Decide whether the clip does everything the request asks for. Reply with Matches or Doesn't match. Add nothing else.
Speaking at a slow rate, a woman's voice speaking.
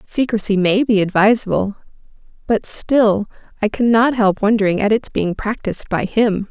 Doesn't match